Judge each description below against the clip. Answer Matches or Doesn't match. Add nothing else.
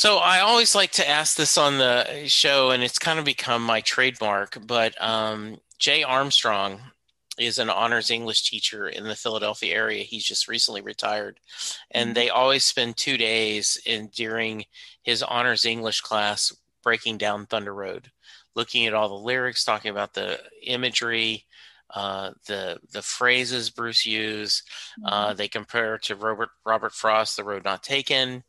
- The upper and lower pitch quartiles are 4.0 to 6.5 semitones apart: Doesn't match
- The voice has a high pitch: Doesn't match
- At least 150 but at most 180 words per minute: Matches